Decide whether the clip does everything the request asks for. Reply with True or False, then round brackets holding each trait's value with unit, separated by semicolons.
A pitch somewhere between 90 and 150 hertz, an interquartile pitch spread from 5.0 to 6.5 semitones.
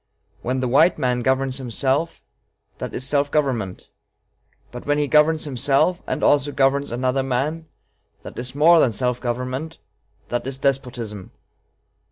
False (135 Hz; 2.7 semitones)